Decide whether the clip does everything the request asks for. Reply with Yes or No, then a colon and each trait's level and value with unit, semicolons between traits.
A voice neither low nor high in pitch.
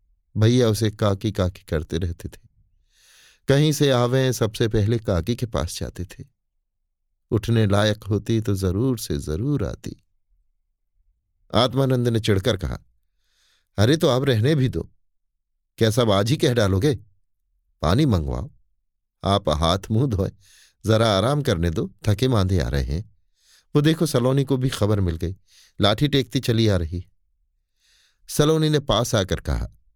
No: low, 105 Hz